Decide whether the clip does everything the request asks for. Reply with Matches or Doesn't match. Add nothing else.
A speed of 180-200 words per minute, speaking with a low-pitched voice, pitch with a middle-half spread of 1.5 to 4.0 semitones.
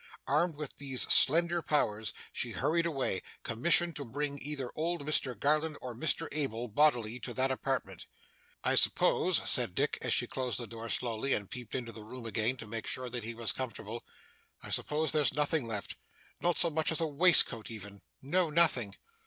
Doesn't match